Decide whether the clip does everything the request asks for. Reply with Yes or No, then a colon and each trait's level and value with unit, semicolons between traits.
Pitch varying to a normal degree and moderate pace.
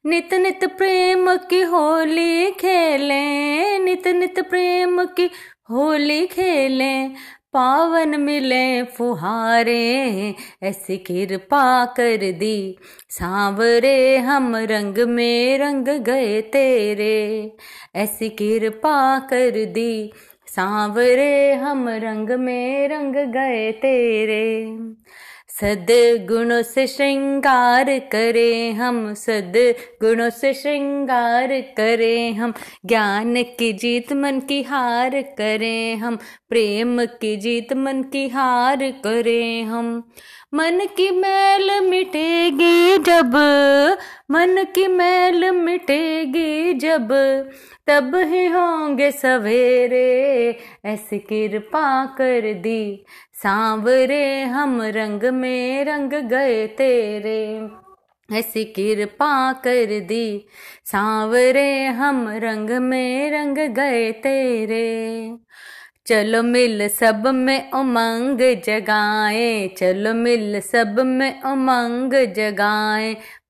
No: average, 4.0 semitones; slow, 90 wpm